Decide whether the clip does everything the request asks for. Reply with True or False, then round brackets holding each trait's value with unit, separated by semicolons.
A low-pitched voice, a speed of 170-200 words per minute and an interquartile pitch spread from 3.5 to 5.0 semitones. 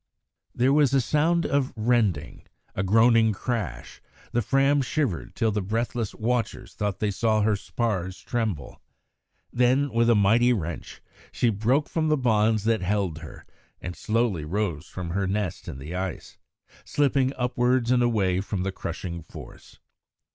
False (110 Hz; 155 wpm; 4.5 semitones)